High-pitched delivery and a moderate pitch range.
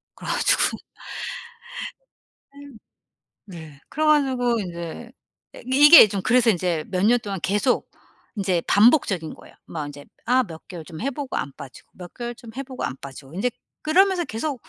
No: high, 210 Hz; wide, 7.2 semitones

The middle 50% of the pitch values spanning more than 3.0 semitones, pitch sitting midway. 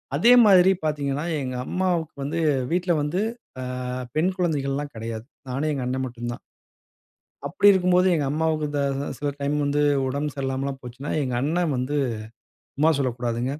Yes: average, 3.6 semitones; medium, 145 Hz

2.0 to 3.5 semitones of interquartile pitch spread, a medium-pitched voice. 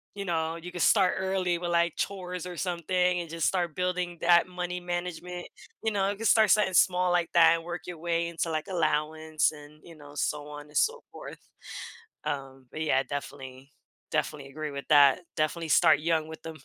Yes: average, 2.7 semitones; medium, 170 Hz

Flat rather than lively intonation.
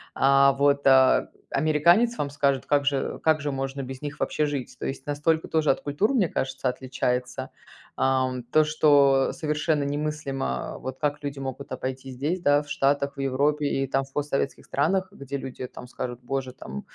Yes: narrow, 2.0 semitones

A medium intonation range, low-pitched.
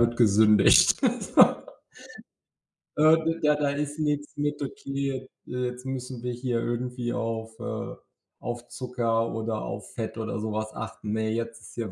Yes: average, 3.1 semitones; low, 120 Hz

